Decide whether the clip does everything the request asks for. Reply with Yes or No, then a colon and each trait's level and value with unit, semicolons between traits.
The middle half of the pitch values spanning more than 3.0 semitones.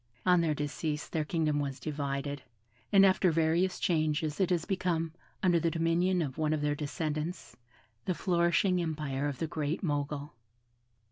No: average, 2.7 semitones